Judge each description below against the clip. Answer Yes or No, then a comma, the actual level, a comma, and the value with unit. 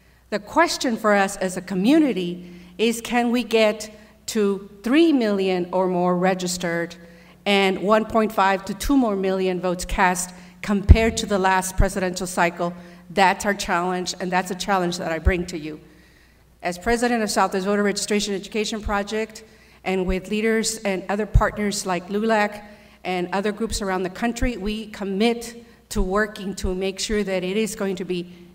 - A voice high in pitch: Yes, high, 195 Hz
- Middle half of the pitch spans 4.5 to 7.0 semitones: No, average, 2.8 semitones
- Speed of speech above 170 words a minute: No, average, 165 wpm